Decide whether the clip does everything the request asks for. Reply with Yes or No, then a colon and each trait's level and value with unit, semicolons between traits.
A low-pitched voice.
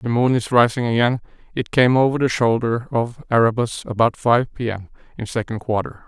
Yes: low, 120 Hz